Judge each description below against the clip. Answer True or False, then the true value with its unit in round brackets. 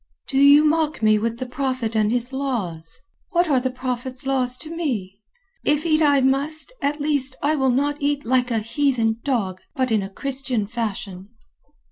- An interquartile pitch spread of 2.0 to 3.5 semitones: False (4.0 semitones)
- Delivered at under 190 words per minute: True (175 wpm)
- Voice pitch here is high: True (260 Hz)